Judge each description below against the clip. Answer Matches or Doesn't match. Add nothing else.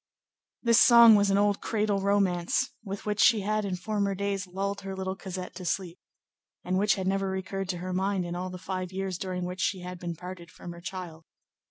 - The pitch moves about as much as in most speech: Doesn't match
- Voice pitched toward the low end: Doesn't match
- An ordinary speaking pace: Doesn't match